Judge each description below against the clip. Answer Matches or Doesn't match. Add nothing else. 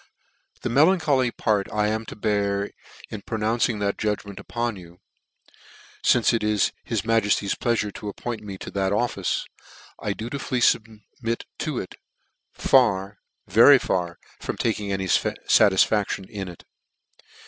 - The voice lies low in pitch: Matches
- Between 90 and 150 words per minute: Matches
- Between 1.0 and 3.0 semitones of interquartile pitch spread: Matches